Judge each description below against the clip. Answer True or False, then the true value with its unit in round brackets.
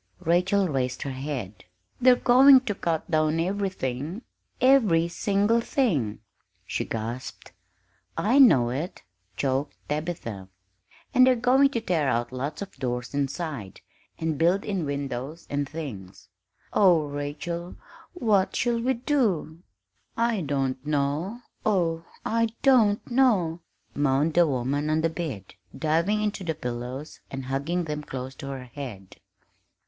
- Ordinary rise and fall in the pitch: False (7.0 semitones)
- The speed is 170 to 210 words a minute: False (135 wpm)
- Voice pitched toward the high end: False (160 Hz)